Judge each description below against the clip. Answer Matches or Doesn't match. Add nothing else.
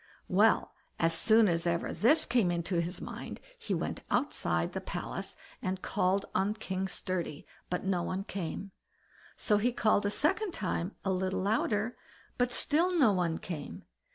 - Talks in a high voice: Matches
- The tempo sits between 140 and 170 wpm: Matches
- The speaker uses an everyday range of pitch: Matches